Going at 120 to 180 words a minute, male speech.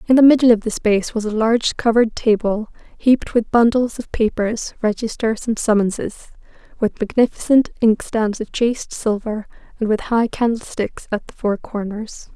No: average, 160 wpm; female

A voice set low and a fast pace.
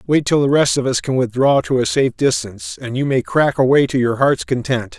Yes: low, 130 Hz; fast, 255 wpm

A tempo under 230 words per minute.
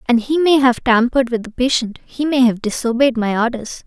Yes: average, 200 wpm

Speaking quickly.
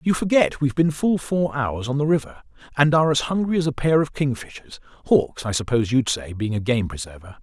Yes: fast, 220 wpm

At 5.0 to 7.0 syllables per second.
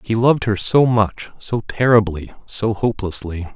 No: 4.6 syllables/s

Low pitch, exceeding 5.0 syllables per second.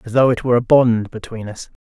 Yes: low, 120 Hz; 6.2 syllables/s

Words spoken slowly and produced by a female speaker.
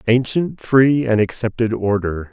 No: slow, 130 wpm; male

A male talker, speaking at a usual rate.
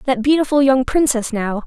No: female; average, 180 wpm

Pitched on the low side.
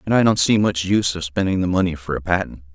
Yes: very low, 90 Hz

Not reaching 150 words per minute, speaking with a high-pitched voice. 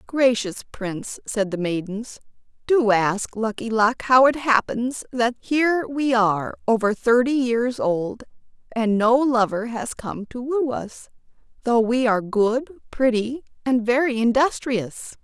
Yes: average, 140 wpm; high, 235 Hz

